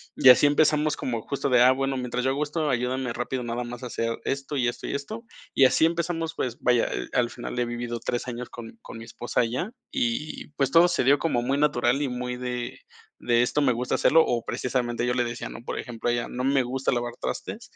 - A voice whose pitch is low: Yes, low, 125 Hz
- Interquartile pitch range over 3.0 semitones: No, narrow, 2.6 semitones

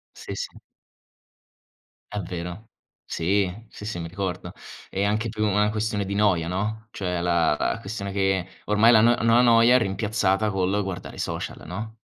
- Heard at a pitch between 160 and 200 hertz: No, low, 100 Hz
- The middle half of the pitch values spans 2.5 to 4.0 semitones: Yes, average, 2.8 semitones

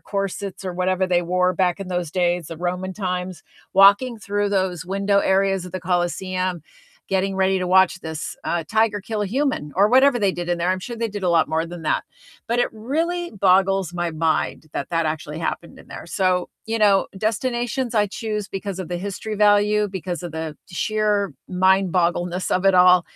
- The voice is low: No, high, 190 Hz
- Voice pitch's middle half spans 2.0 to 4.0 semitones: Yes, narrow, 2.6 semitones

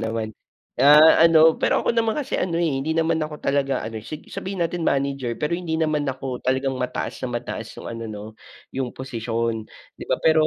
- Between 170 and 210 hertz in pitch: No, medium, 140 Hz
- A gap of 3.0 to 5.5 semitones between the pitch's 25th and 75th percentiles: Yes, average, 4.6 semitones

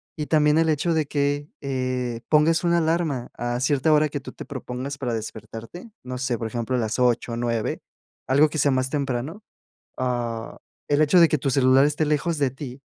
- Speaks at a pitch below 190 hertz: Yes, low, 135 Hz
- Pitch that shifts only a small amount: No, average, 3.6 semitones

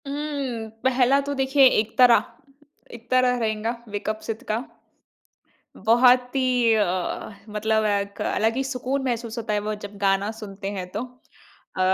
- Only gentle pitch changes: No, average, 3.3 semitones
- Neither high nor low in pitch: No, high, 225 Hz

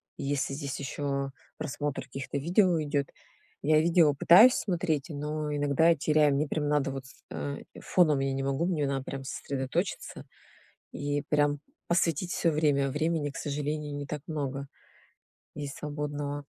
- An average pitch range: No, narrow, 1.8 semitones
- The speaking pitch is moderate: Yes, medium, 145 Hz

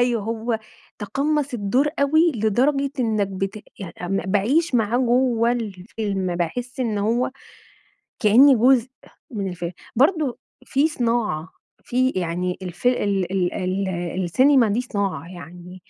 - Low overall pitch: No, high, 225 Hz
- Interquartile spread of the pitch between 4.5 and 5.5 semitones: Yes, average, 4.8 semitones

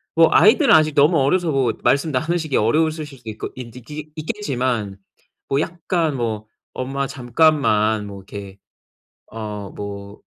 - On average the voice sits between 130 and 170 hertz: Yes, low, 135 Hz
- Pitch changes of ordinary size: No, wide, 6.4 semitones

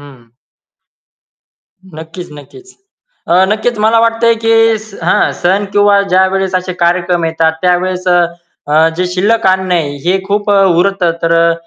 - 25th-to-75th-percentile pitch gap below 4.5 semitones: Yes, average, 2.9 semitones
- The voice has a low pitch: No, medium, 185 Hz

